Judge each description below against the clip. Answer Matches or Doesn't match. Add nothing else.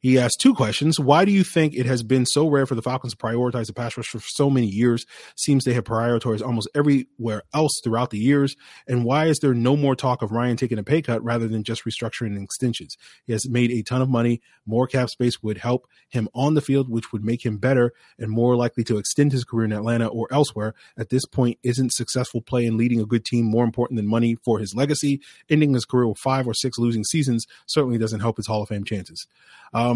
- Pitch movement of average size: Doesn't match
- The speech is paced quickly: Matches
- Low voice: Matches